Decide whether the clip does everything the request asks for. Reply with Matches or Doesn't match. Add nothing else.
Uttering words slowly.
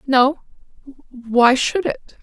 Matches